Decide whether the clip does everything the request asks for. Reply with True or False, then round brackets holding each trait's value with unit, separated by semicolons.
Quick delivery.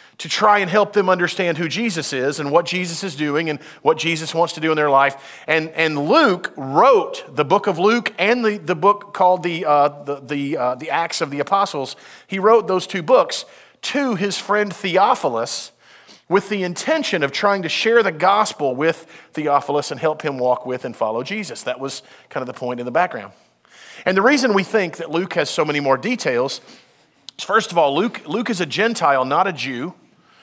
True (210 wpm)